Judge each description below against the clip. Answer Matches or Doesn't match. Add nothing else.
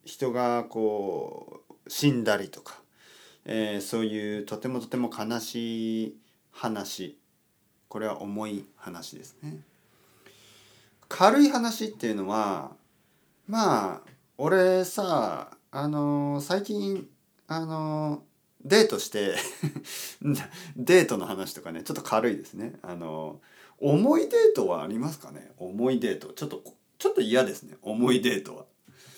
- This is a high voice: Doesn't match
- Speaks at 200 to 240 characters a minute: Matches